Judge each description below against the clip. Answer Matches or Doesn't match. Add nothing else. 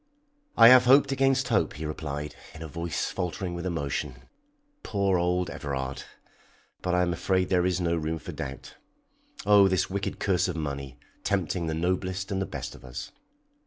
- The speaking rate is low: Doesn't match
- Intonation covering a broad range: Doesn't match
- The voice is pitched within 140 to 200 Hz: Doesn't match